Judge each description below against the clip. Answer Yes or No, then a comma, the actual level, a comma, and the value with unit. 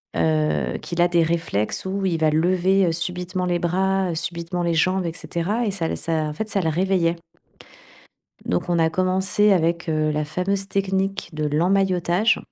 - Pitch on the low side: No, medium, 175 Hz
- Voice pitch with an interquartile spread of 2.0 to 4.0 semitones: Yes, average, 2.8 semitones